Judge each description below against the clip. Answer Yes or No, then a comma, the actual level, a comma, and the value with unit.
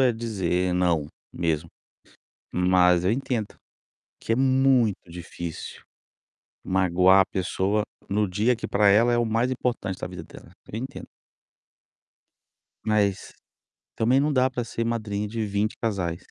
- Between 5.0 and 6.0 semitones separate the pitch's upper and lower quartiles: No, average, 4.4 semitones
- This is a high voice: No, low, 105 Hz